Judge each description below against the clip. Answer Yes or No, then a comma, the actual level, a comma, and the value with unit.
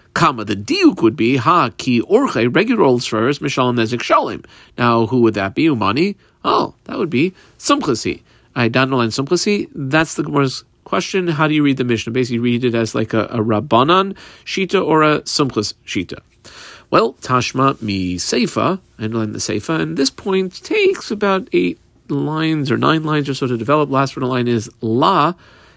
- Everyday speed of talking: Yes, average, 185 wpm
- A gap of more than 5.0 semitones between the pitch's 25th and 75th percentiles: Yes, wide, 5.5 semitones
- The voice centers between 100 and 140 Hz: Yes, low, 135 Hz